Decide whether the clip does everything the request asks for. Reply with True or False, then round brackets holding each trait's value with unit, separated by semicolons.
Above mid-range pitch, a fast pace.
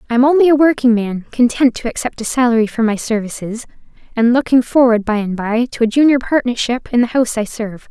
True (240 Hz; 220 wpm)